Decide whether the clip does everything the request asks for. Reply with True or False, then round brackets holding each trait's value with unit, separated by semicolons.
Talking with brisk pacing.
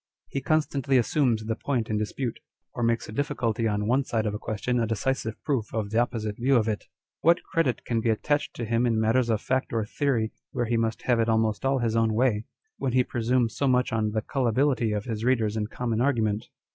True (225 wpm)